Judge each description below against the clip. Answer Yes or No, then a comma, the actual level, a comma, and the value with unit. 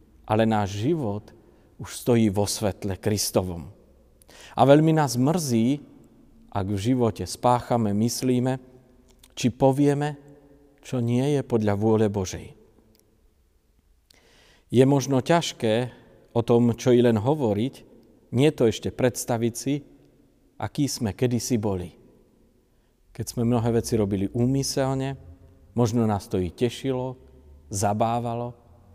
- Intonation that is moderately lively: Yes, average, 4.0 semitones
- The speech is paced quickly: No, average, 115 wpm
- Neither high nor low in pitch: No, low, 115 Hz